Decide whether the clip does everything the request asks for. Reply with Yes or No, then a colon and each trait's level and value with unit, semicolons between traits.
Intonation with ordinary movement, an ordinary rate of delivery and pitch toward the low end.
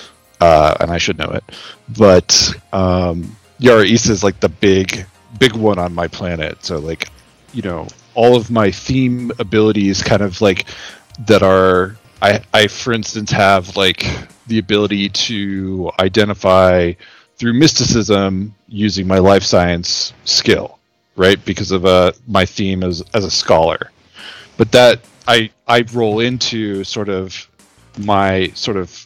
Yes: average, 3.4 semitones; average, 145 wpm; low, 100 Hz